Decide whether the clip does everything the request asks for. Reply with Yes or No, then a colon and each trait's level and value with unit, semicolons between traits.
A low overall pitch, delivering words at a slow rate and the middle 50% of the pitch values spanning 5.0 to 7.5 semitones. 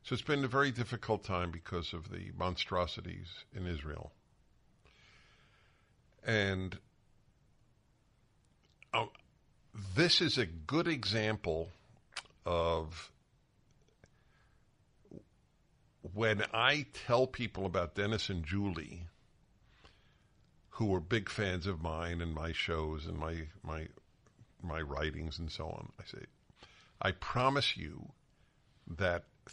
Yes: low, 100 Hz; slow, 105 wpm; wide, 5.6 semitones